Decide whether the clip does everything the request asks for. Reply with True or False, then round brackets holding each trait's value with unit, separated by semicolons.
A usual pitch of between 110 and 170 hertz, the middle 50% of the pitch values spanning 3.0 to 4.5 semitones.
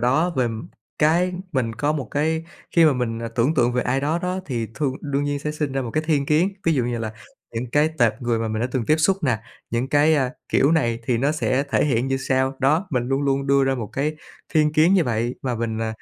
True (135 Hz; 4.1 semitones)